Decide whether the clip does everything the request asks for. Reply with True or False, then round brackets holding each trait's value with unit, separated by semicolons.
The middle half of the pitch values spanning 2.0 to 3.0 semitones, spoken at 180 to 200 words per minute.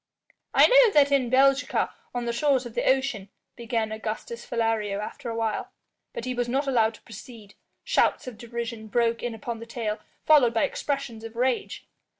True (2.6 semitones; 185 wpm)